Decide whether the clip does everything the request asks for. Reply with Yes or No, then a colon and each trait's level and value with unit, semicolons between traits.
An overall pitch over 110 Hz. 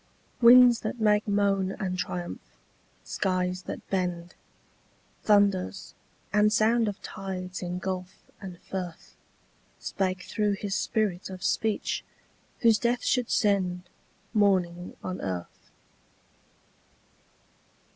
Yes: high, 190 Hz